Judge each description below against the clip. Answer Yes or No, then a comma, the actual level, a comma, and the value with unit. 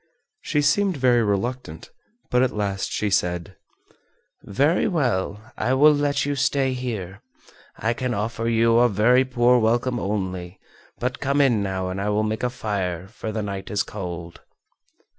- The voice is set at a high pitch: No, low, 115 Hz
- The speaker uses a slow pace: No, average, 160 wpm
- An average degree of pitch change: Yes, average, 4.6 semitones